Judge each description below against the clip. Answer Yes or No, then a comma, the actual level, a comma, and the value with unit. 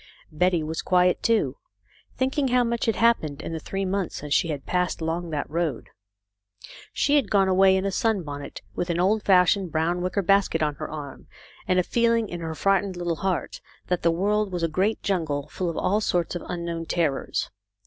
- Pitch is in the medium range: Yes, medium, 180 Hz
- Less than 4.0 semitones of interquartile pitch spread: Yes, average, 3.4 semitones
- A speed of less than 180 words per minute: No, average, 200 wpm